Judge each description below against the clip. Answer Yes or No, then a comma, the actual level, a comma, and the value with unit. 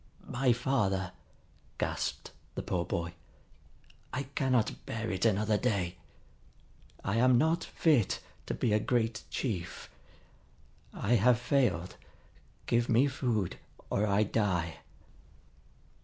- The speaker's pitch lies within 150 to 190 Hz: No, low, 110 Hz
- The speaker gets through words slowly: Yes, slow, 110 wpm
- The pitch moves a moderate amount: Yes, average, 4.4 semitones